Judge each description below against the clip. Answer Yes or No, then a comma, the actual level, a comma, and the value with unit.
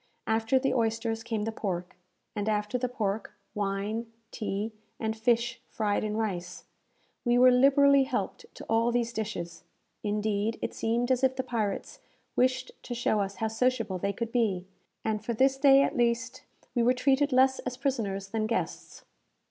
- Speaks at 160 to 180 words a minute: Yes, average, 170 wpm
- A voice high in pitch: Yes, high, 230 Hz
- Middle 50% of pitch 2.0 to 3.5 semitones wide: Yes, average, 3.2 semitones